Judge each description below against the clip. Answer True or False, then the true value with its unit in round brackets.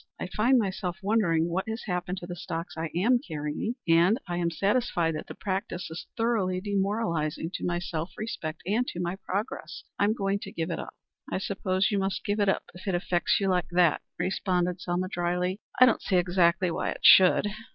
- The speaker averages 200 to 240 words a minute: True (205 wpm)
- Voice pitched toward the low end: False (185 Hz)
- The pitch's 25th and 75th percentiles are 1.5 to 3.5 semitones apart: True (2.6 semitones)